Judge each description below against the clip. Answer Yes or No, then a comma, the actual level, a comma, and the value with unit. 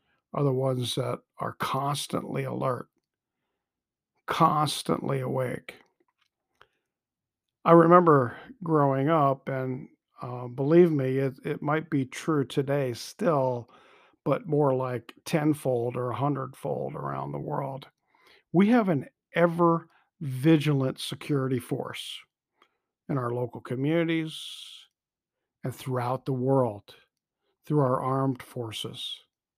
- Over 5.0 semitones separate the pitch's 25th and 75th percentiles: No, average, 3.4 semitones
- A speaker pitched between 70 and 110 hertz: No, medium, 140 Hz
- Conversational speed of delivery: No, slow, 110 wpm